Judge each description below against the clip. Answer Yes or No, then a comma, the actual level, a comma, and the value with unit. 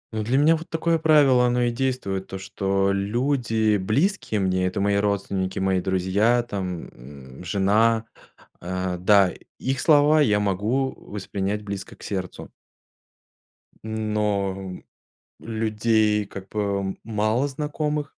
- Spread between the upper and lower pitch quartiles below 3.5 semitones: No, average, 4.2 semitones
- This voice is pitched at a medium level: No, low, 105 Hz